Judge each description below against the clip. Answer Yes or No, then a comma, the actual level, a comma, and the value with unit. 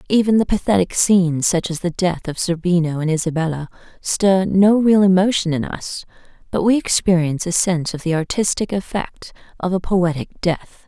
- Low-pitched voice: No, medium, 180 Hz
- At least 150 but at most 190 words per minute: Yes, average, 170 wpm